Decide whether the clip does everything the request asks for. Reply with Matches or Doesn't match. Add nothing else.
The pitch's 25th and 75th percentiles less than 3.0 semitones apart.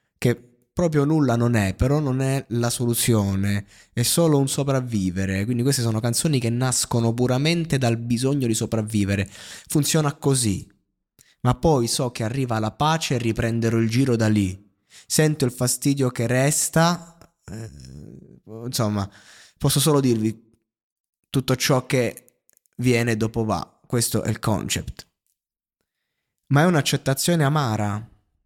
Doesn't match